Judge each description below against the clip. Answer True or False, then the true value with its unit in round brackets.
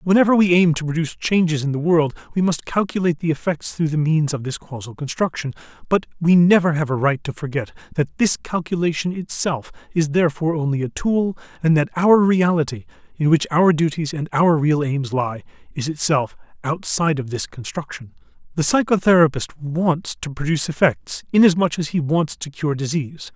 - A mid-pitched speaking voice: True (160 Hz)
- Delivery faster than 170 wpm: True (180 wpm)